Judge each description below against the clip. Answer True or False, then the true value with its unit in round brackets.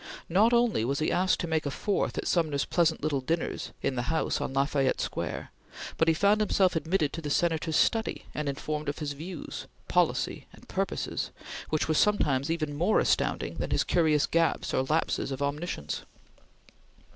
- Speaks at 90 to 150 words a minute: False (180 wpm)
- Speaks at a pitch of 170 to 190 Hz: False (155 Hz)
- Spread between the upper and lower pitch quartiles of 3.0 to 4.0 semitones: True (3.3 semitones)